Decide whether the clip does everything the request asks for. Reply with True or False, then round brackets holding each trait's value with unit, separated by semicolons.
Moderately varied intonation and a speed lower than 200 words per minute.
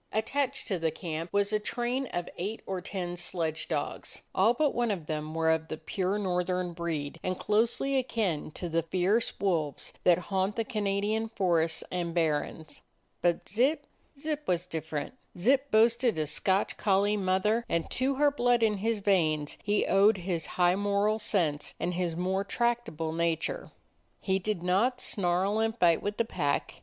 True (4.6 semitones; 170 wpm)